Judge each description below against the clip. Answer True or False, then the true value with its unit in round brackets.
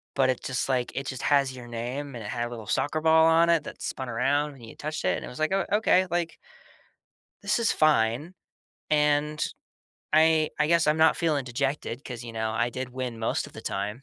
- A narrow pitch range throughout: False (4.3 semitones)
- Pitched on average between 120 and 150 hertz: True (140 Hz)